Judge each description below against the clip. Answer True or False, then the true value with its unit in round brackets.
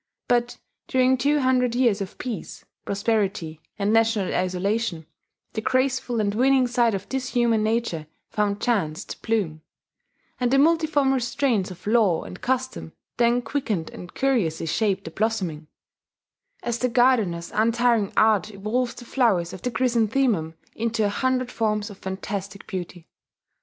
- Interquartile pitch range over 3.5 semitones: True (4.2 semitones)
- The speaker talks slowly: False (145 wpm)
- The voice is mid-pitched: False (225 Hz)